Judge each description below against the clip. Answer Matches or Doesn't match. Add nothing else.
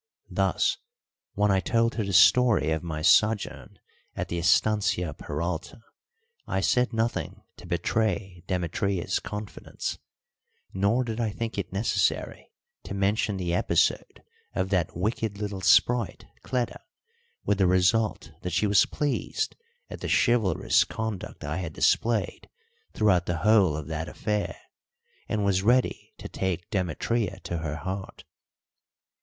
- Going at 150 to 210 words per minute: Doesn't match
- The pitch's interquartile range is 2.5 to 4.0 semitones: Matches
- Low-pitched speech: Matches